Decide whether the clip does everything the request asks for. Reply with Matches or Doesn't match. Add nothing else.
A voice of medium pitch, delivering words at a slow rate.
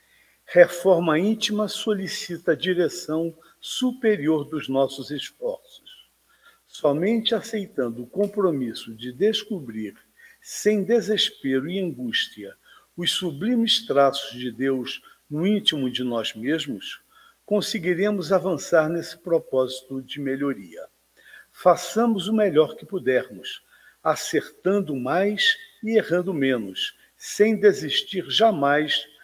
Matches